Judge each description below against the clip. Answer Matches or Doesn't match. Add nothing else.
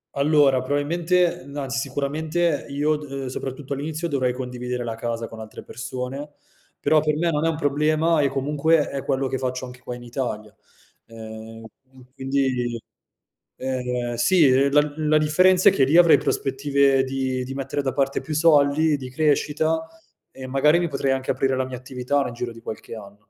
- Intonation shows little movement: Doesn't match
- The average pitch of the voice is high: Doesn't match